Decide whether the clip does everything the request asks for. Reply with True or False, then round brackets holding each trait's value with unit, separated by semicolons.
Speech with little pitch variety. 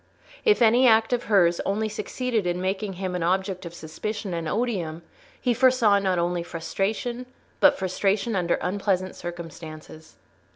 False (4.1 semitones)